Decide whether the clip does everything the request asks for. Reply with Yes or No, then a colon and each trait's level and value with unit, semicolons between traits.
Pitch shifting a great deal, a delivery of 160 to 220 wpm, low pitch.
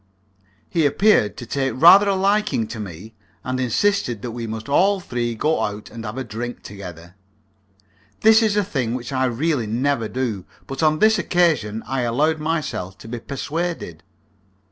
Yes: wide, 6.6 semitones; average, 170 wpm; low, 130 Hz